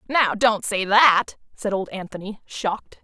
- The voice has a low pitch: No, high, 210 Hz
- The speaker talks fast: No, average, 160 wpm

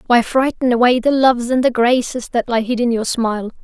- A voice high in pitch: Yes, high, 240 Hz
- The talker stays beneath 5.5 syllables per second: No, 5.6 syllables/s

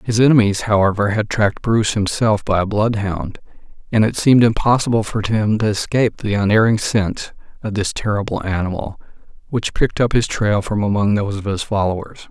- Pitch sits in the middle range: No, low, 105 Hz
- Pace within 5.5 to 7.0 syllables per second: Yes, 5.6 syllables/s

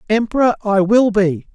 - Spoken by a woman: No, male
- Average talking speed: Yes, average, 155 wpm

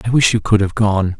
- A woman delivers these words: No, male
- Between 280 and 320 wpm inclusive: Yes, fast, 300 wpm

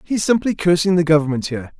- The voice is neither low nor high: Yes, medium, 170 Hz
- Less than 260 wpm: Yes, average, 200 wpm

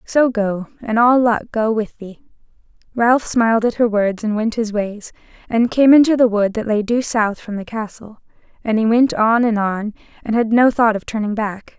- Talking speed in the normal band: No, fast, 215 wpm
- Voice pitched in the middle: No, high, 225 Hz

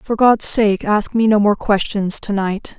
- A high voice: Yes, high, 210 Hz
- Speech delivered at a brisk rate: Yes, fast, 215 wpm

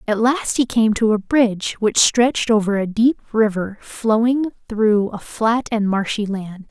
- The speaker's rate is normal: Yes, average, 180 wpm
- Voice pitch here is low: No, high, 220 Hz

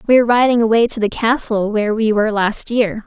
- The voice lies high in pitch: Yes, high, 220 Hz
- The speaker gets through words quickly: Yes, fast, 235 wpm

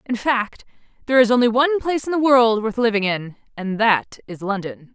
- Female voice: Yes, female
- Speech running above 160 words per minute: Yes, fast, 205 wpm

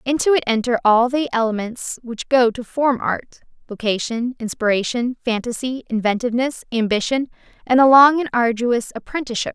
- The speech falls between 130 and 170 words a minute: Yes, average, 150 wpm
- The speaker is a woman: Yes, female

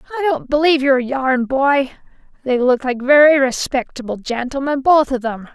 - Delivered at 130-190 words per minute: Yes, average, 150 wpm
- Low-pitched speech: No, very high, 265 Hz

